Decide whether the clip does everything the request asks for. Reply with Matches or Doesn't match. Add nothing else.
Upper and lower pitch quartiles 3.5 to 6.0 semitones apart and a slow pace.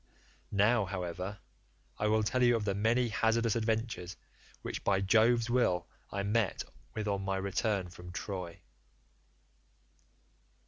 Doesn't match